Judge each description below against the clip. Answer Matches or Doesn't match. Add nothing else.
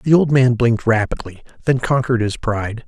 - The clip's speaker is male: Matches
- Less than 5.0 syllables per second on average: Doesn't match